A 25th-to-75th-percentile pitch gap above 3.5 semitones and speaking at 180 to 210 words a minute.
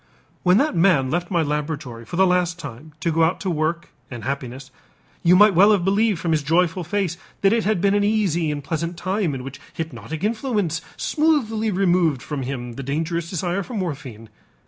Yes: average, 4.7 semitones; average, 195 wpm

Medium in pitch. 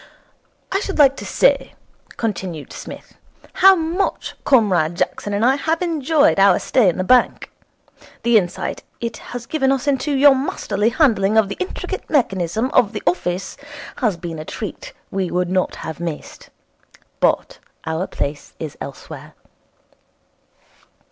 No: high, 220 Hz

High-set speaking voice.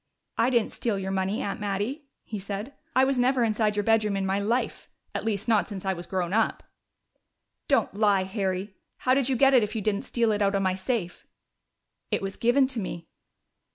Yes: high, 210 Hz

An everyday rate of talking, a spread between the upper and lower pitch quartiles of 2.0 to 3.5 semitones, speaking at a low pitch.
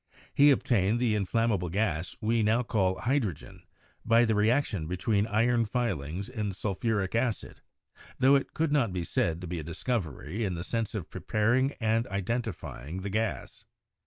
No: average, 170 wpm; average, 4.0 semitones; low, 110 Hz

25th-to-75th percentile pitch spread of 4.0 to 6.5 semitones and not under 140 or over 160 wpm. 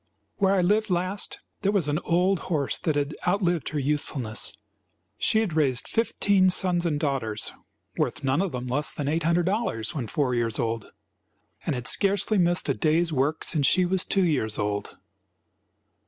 No: wide, 5.5 semitones; average, 170 wpm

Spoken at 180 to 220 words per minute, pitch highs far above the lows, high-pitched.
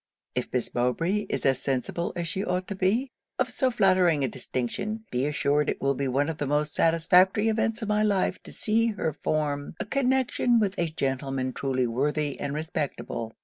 No: average, 190 wpm; wide, 6.9 semitones; medium, 160 Hz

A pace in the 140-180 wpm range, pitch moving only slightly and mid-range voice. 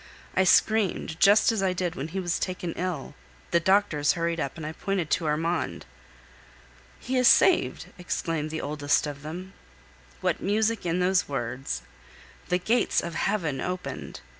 No: average, 160 wpm; average, 3.8 semitones; medium, 175 Hz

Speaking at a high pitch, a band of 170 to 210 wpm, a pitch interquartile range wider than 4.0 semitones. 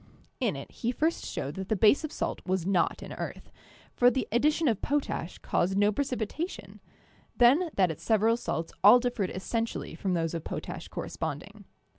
Yes: high, 220 Hz; average, 175 wpm; average, 5.1 semitones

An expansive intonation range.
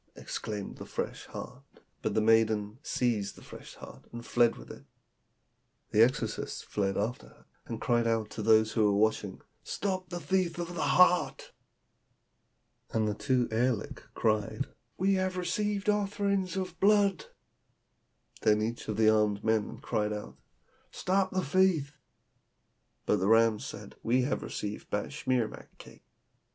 Yes: wide, 9.0 semitones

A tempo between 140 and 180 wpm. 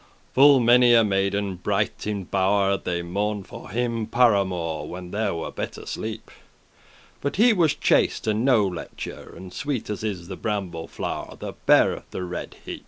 Yes: average, 170 wpm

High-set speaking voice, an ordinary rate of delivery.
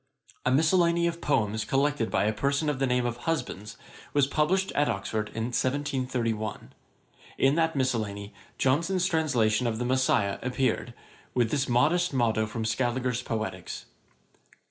No: low, 130 Hz; average, 145 wpm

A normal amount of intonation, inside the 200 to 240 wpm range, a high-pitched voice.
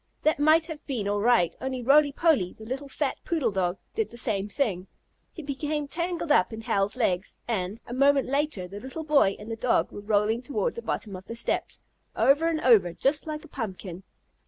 No: wide, 6.5 semitones; fast, 205 wpm; very high, 255 Hz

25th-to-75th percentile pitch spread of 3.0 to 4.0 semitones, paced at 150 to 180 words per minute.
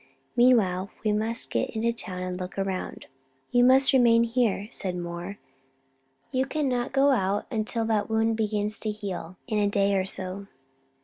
Yes: average, 3.5 semitones; average, 165 wpm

